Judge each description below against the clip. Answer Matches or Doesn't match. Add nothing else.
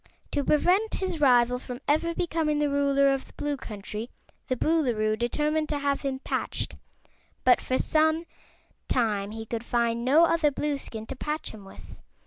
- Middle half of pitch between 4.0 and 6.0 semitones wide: Matches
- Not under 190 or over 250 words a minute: Doesn't match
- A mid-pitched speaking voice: Doesn't match